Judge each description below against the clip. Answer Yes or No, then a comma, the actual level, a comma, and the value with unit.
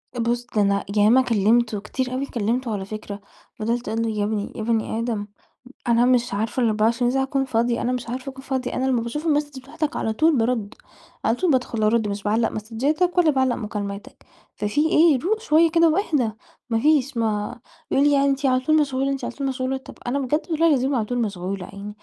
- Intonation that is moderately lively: Yes, average, 3.9 semitones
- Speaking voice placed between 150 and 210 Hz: No, high, 245 Hz